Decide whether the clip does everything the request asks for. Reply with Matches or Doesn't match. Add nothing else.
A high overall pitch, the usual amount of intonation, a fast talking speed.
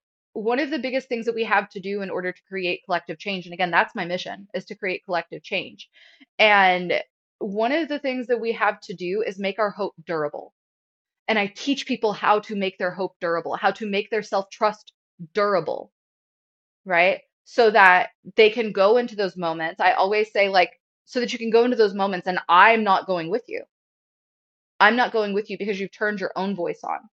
Matches